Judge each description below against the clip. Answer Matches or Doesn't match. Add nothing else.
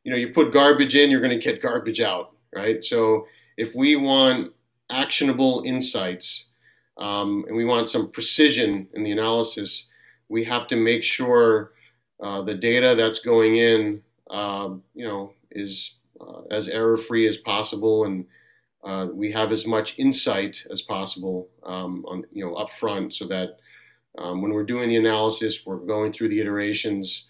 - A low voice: Matches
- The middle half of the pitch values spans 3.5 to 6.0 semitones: Doesn't match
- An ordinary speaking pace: Matches